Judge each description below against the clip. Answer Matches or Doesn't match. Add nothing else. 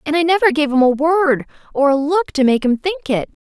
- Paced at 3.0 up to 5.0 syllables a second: Doesn't match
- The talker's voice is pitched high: Matches